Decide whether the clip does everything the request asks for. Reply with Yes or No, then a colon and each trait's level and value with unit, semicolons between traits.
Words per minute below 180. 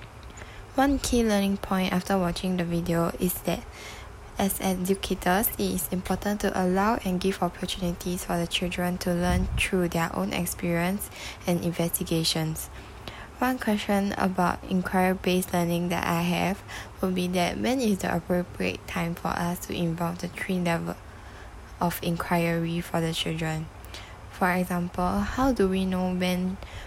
Yes: average, 150 wpm